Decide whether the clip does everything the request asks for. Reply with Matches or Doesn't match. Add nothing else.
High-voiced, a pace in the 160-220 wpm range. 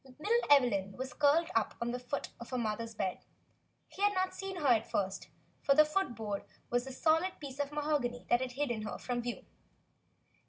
Matches